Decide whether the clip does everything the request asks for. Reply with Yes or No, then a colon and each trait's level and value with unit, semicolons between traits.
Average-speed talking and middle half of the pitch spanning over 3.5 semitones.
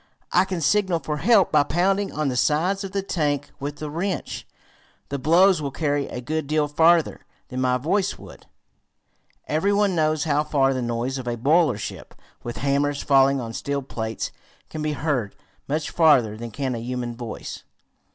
Yes: average, 180 wpm; average, 4.2 semitones